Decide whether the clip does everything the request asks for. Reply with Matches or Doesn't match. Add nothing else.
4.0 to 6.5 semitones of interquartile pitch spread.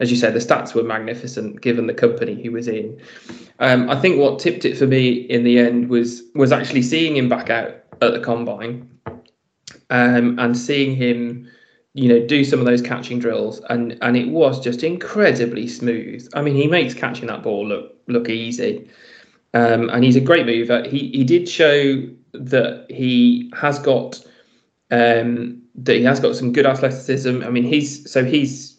Doesn't match